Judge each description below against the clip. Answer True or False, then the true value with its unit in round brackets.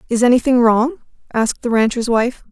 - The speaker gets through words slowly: False (165 wpm)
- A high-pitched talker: True (240 Hz)